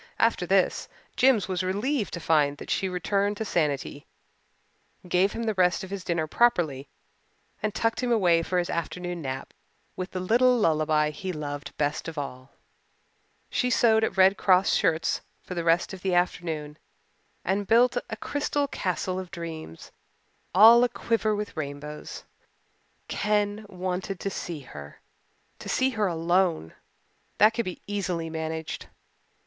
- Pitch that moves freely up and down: No, average, 4.6 semitones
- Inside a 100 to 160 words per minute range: Yes, average, 155 wpm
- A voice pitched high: No, medium, 180 Hz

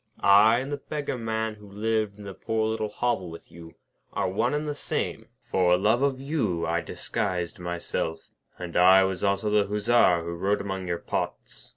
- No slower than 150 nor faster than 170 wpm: No, average, 190 wpm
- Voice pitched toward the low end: Yes, low, 100 Hz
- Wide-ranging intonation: No, average, 3.8 semitones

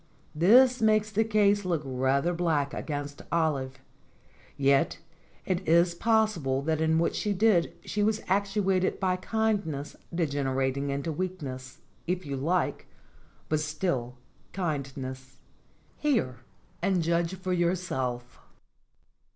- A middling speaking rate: No, slow, 120 wpm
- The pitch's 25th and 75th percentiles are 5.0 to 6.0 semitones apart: Yes, wide, 5.6 semitones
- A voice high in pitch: No, medium, 170 Hz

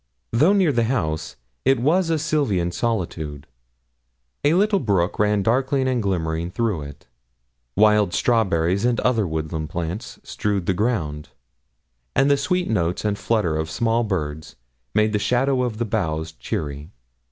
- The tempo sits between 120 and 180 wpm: Yes, average, 150 wpm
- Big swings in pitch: Yes, wide, 7.1 semitones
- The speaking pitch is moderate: No, low, 105 Hz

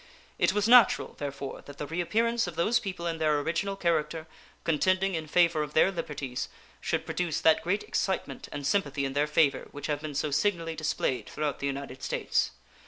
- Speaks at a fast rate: No, average, 185 wpm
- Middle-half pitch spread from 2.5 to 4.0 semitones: Yes, average, 3.7 semitones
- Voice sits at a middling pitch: Yes, medium, 160 Hz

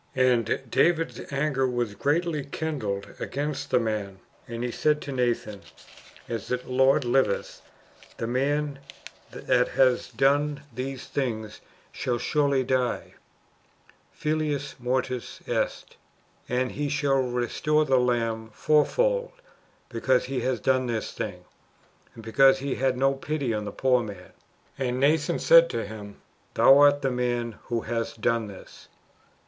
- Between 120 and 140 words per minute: Yes, slow, 135 wpm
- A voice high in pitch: No, low, 130 Hz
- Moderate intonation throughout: Yes, average, 3.3 semitones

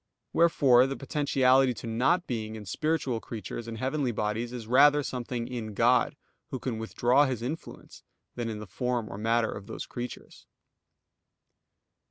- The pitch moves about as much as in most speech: Yes, average, 3.0 semitones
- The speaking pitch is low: Yes, low, 120 Hz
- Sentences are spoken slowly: No, average, 155 wpm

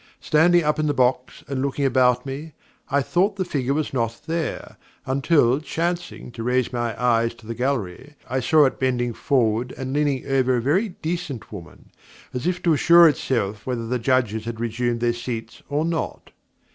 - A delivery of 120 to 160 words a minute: No, average, 185 wpm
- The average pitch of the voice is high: No, low, 130 Hz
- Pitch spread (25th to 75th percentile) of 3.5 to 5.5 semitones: Yes, average, 4.1 semitones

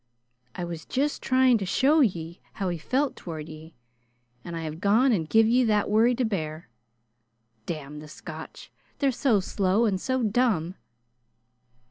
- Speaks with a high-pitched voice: Yes, high, 200 Hz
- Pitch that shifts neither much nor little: No, wide, 7.1 semitones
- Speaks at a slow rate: No, average, 155 wpm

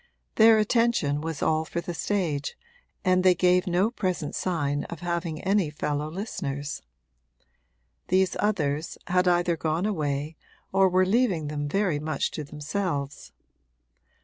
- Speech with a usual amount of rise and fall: Yes, average, 4.0 semitones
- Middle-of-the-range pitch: Yes, medium, 170 Hz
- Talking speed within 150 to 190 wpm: No, slow, 135 wpm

